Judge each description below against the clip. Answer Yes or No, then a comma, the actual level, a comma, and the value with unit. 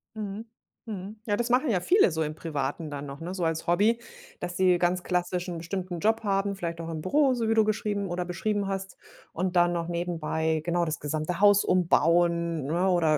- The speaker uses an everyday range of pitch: Yes, average, 3.4 semitones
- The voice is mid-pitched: Yes, medium, 175 Hz